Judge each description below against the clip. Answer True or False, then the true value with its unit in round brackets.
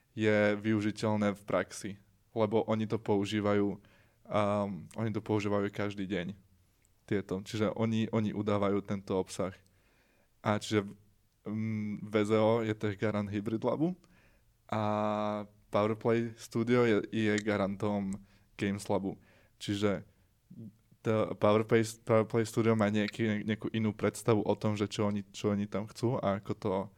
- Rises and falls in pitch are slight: True (1.4 semitones)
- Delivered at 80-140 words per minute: True (135 wpm)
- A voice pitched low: True (105 Hz)